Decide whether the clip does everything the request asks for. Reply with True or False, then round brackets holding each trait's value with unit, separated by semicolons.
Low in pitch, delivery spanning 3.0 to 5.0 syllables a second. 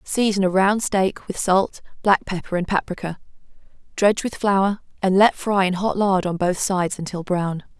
False (190 Hz; 4.8 syllables/s)